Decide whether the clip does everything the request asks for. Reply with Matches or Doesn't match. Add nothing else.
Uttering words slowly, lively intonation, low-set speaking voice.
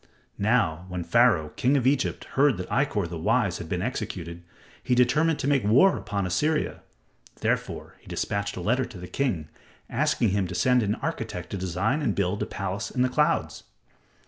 Doesn't match